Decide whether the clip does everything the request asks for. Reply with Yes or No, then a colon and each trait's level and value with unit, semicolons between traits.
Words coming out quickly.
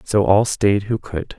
Yes: fast, 215 wpm